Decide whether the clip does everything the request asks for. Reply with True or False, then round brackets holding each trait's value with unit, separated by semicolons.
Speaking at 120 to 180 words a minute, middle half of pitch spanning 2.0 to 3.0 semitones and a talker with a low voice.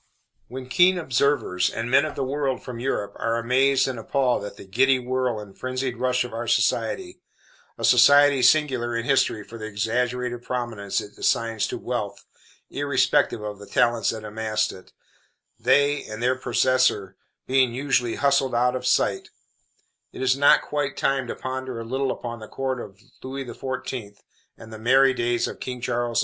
True (175 wpm; 2.6 semitones; 125 Hz)